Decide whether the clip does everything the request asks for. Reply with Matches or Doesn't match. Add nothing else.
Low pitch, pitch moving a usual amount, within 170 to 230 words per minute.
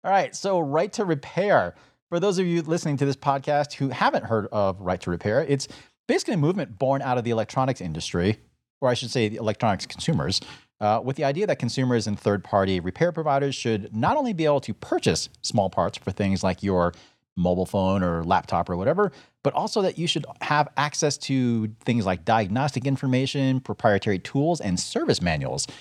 Doesn't match